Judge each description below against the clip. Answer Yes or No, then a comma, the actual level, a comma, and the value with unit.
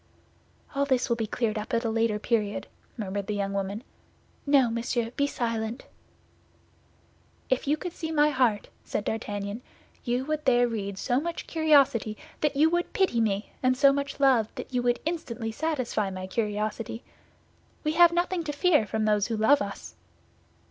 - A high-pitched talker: Yes, high, 240 Hz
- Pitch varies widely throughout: No, average, 4.8 semitones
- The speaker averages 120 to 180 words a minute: Yes, average, 170 wpm